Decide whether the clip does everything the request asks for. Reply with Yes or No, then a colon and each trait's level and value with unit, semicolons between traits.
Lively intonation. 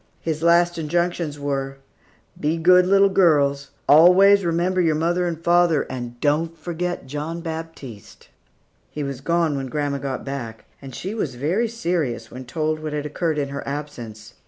No: average, 3.7 semitones